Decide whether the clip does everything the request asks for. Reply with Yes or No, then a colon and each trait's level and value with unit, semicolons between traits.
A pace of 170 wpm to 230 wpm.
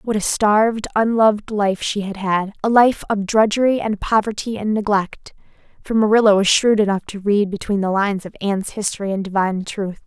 Yes: average, 190 wpm